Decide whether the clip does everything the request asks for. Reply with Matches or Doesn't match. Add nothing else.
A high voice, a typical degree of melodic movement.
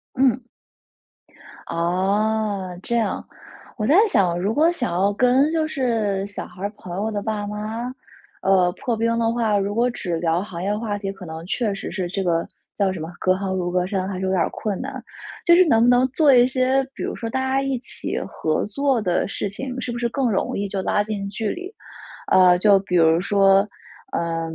Matches